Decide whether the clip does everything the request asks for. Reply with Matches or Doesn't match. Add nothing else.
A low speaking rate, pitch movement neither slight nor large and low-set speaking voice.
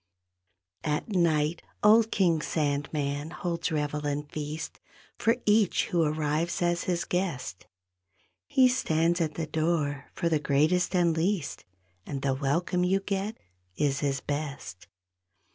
Doesn't match